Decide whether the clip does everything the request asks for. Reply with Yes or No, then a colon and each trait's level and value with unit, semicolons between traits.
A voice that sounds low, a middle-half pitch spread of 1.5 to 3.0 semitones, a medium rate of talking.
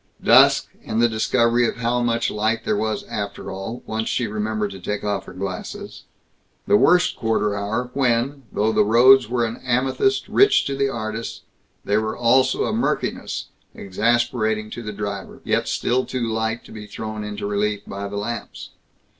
Yes: low, 110 Hz; narrow, 2.6 semitones; average, 175 wpm